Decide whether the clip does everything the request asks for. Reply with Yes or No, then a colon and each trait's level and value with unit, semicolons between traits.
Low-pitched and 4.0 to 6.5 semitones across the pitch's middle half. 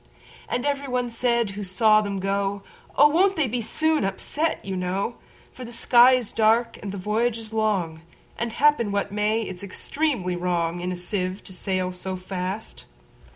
No: high, 210 Hz; average, 4.3 semitones